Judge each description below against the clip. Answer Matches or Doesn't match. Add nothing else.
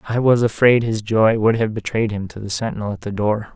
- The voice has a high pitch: Doesn't match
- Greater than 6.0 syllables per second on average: Doesn't match